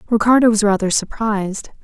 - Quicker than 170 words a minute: No, slow, 130 wpm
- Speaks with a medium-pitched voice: No, high, 215 Hz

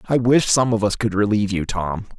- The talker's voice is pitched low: Yes, low, 105 Hz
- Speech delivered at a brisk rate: Yes, fast, 245 wpm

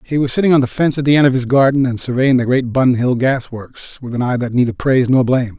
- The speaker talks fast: Yes, fast, 300 wpm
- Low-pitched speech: Yes, low, 130 Hz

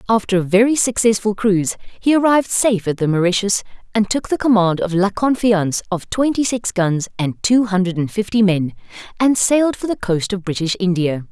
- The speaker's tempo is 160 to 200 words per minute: Yes, average, 190 wpm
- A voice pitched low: No, high, 205 Hz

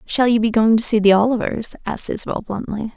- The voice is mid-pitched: No, high, 225 Hz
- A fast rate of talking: Yes, fast, 225 wpm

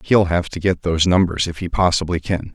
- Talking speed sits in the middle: No, fast, 235 wpm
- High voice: No, very low, 85 Hz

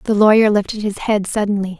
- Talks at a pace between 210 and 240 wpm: No, average, 200 wpm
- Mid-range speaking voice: No, high, 205 Hz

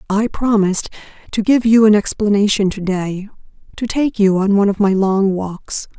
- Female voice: Yes, female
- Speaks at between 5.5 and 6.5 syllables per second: No, 5.0 syllables/s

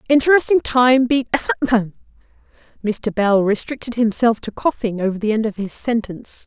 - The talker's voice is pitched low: No, high, 235 Hz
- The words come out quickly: No, average, 140 wpm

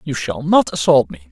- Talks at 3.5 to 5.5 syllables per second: Yes, 5.4 syllables/s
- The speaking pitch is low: Yes, low, 125 Hz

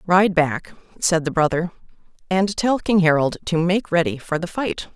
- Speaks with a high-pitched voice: No, medium, 175 Hz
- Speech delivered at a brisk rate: No, average, 180 wpm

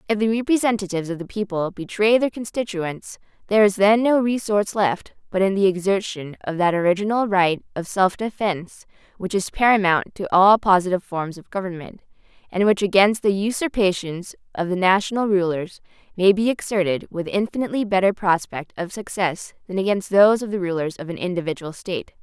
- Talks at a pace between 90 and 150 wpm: No, average, 170 wpm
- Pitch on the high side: Yes, high, 195 Hz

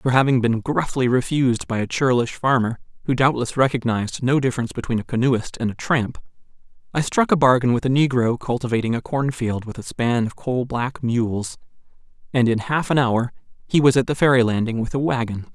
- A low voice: Yes, low, 125 Hz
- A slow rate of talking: No, average, 195 wpm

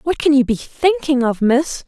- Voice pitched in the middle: No, very high, 280 Hz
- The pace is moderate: No, fast, 225 wpm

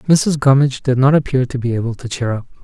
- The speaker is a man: Yes, male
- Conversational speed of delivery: No, fast, 250 wpm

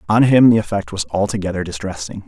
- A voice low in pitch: Yes, low, 100 Hz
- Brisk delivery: No, average, 185 wpm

